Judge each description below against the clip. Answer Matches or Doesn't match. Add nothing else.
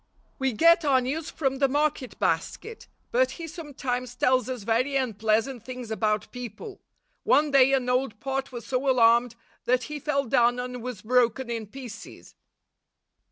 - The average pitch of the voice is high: Matches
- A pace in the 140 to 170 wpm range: Matches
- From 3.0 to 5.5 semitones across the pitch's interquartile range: Doesn't match